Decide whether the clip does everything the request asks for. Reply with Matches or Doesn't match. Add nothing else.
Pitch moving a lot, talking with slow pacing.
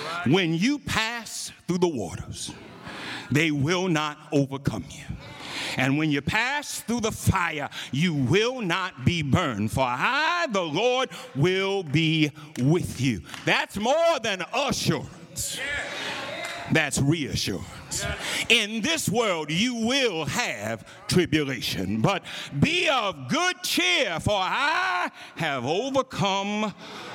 Matches